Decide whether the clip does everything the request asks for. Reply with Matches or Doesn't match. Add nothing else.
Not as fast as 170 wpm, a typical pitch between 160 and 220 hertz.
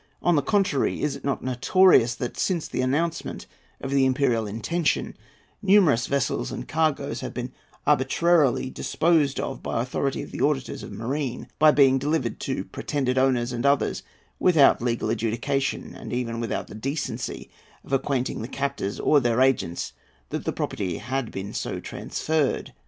Doesn't match